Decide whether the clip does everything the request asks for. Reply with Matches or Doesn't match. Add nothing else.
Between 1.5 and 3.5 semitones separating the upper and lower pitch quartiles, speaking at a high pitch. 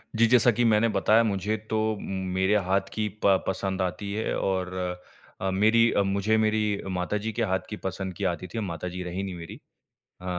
Doesn't match